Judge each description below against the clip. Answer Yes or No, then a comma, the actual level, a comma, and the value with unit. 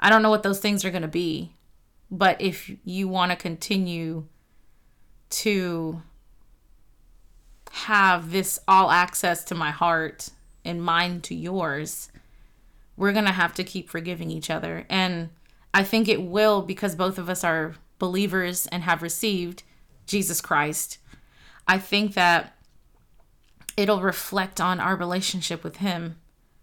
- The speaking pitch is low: No, medium, 180 Hz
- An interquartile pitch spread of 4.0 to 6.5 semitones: No, narrow, 2.4 semitones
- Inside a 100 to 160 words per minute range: Yes, average, 140 wpm